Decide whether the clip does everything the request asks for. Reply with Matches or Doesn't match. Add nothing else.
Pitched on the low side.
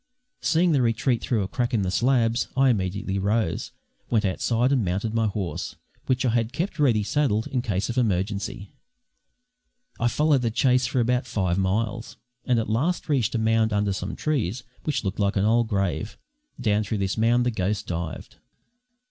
Matches